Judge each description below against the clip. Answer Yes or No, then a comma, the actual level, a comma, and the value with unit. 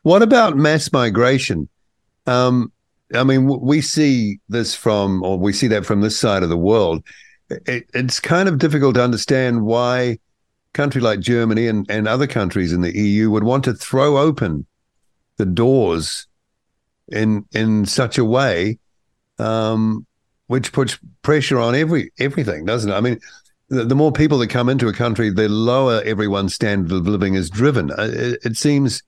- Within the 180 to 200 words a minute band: No, average, 170 wpm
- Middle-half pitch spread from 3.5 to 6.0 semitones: Yes, average, 3.8 semitones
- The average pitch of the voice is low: Yes, low, 120 Hz